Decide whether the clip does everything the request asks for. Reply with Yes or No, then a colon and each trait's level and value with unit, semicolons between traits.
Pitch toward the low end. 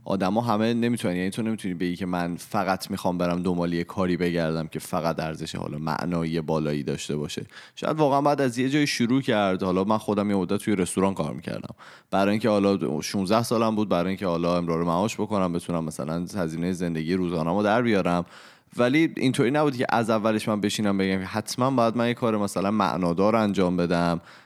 Yes: very low, 95 Hz